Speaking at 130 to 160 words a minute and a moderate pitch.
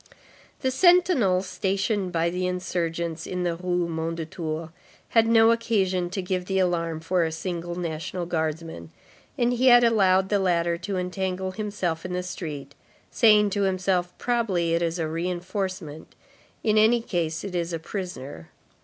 Yes: average, 155 wpm; medium, 180 Hz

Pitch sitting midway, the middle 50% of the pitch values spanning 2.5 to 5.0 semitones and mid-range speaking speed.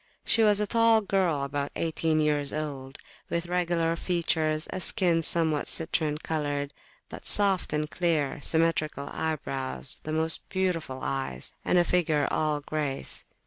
Yes: medium, 160 Hz; average, 2.9 semitones; average, 145 wpm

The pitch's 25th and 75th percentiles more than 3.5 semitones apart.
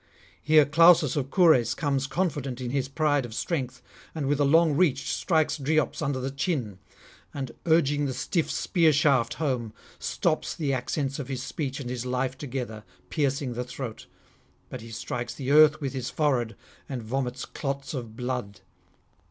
No: average, 3.1 semitones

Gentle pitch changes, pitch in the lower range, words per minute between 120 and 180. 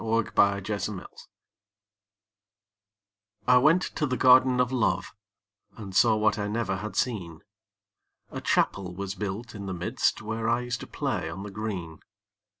No: average, 3.8 semitones; low, 105 Hz; average, 155 wpm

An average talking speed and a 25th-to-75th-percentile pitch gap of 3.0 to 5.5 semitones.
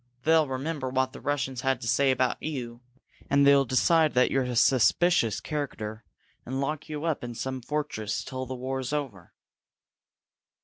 No: average, 165 wpm; narrow, 2.6 semitones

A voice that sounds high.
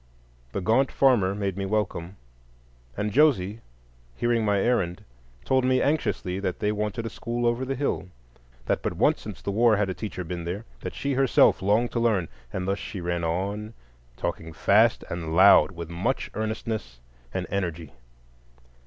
No: low, 100 Hz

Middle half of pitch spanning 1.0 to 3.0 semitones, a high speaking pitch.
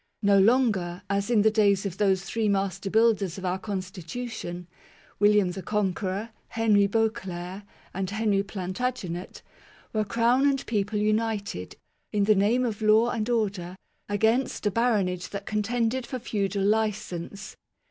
Yes: narrow, 2.6 semitones; high, 205 Hz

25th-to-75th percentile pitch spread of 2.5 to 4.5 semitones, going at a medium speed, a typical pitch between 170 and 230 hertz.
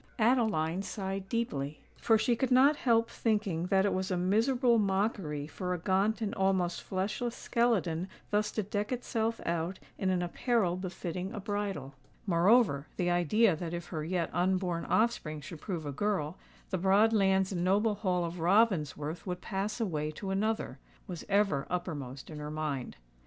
Yes: average, 4.0 semitones; average, 160 wpm; high, 190 Hz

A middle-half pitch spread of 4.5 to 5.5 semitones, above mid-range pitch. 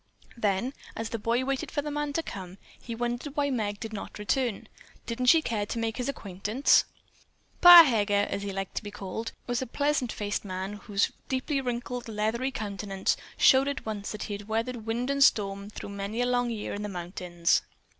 No: average, 3.8 semitones; high, 225 Hz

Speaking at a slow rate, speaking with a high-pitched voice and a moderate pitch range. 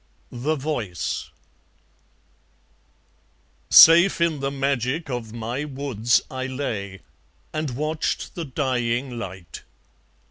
No: slow, 95 wpm; low, 130 Hz; average, 4.1 semitones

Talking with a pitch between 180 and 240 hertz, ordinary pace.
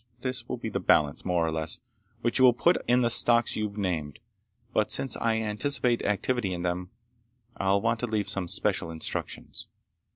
No: low, 105 Hz; average, 185 wpm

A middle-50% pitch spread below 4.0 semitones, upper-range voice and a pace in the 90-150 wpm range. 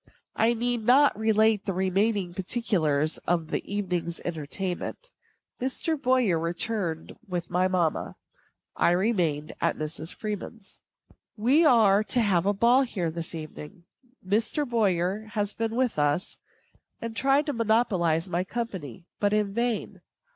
No: average, 5.0 semitones; high, 200 Hz; average, 140 wpm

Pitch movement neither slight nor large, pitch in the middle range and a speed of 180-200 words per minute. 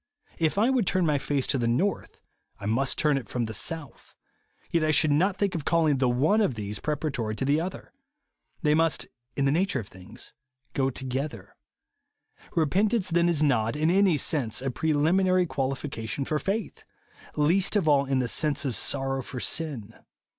Yes: average, 4.4 semitones; medium, 150 Hz; average, 190 wpm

